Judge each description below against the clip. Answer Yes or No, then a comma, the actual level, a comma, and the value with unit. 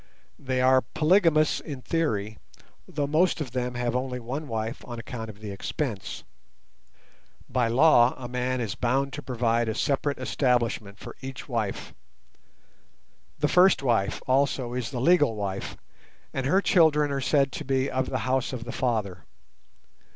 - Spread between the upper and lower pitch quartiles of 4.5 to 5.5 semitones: No, average, 3.4 semitones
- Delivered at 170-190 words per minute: No, average, 160 wpm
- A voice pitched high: No, low, 130 Hz